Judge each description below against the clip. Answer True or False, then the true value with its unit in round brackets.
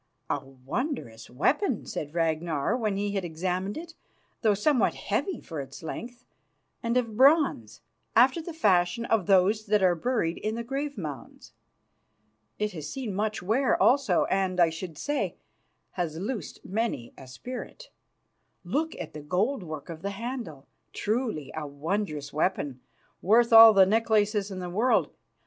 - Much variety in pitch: True (6.5 semitones)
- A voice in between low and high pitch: False (200 Hz)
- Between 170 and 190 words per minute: False (155 wpm)